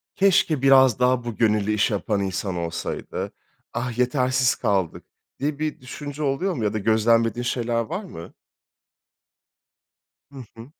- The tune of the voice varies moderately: Yes, average, 4.0 semitones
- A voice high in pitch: No, low, 120 Hz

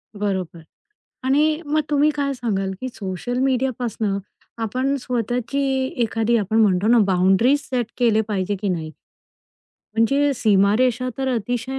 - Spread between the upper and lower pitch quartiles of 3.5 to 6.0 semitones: Yes, average, 4.6 semitones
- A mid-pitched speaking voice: No, high, 235 Hz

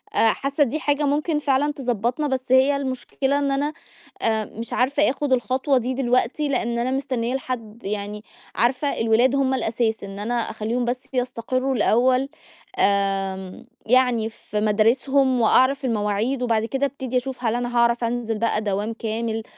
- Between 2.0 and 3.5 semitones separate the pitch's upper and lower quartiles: Yes, average, 3.1 semitones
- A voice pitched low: No, high, 245 Hz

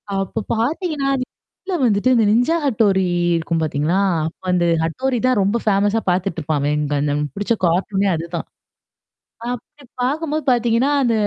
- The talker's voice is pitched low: No, high, 205 Hz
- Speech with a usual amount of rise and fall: No, wide, 6.8 semitones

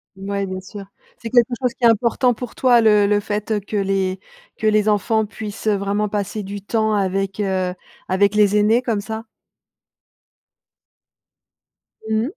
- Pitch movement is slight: Yes, narrow, 1.9 semitones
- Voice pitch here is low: No, high, 210 Hz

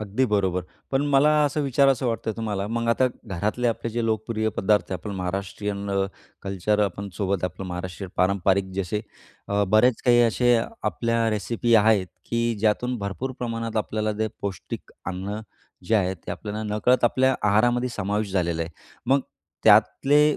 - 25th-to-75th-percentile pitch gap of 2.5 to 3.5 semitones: Yes, average, 3.2 semitones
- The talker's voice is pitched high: No, low, 105 Hz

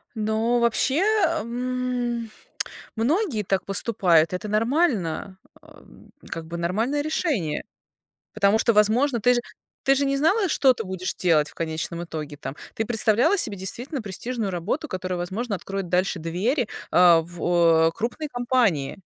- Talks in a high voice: Yes, high, 215 Hz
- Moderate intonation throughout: No, wide, 5.9 semitones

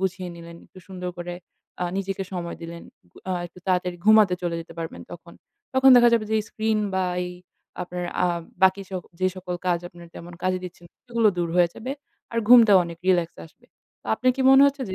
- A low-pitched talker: No, medium, 185 Hz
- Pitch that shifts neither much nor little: Yes, average, 3.7 semitones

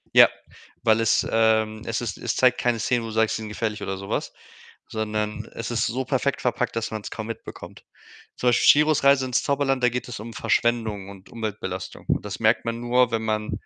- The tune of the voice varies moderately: No, narrow, 2.3 semitones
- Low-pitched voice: Yes, low, 115 Hz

